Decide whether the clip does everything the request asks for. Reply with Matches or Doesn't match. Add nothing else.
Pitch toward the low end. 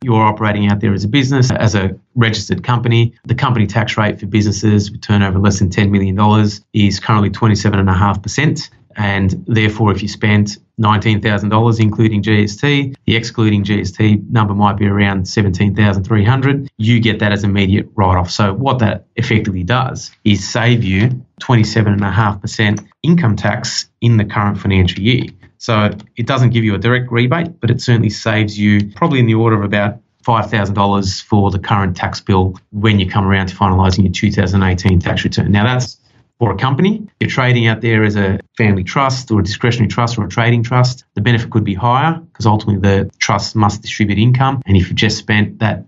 Matches